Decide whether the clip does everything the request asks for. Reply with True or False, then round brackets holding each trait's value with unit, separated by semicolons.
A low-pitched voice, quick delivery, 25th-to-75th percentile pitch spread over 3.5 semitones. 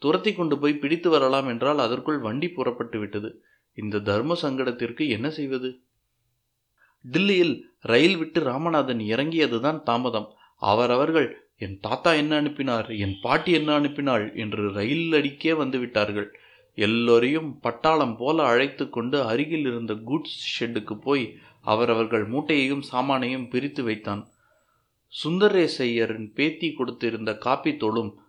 False (130 Hz; 110 wpm; 4.9 semitones)